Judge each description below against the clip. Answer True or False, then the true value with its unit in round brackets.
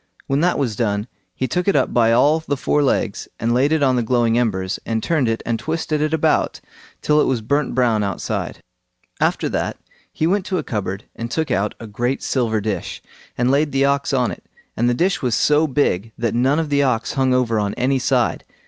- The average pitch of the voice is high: False (125 Hz)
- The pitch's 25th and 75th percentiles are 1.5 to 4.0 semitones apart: False (4.5 semitones)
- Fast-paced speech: True (220 wpm)